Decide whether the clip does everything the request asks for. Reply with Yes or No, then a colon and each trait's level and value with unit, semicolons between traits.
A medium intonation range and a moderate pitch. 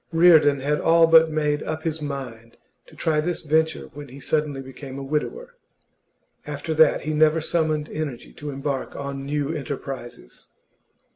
No: narrow, 2.3 semitones; medium, 150 Hz